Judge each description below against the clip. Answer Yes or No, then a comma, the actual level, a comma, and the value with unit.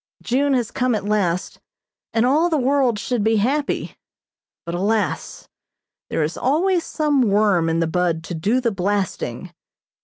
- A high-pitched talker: Yes, high, 220 Hz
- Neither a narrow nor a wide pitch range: No, wide, 6.6 semitones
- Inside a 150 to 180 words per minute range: Yes, average, 155 wpm